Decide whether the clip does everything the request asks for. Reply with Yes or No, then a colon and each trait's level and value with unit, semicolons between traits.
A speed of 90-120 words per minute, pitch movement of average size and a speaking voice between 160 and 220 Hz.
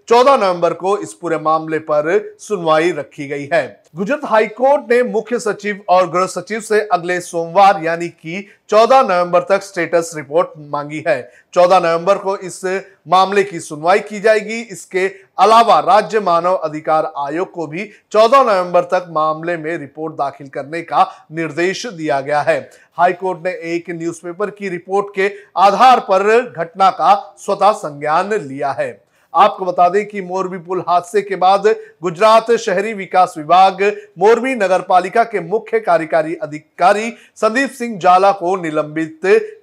No: average, 150 wpm; average, 3.8 semitones; medium, 185 Hz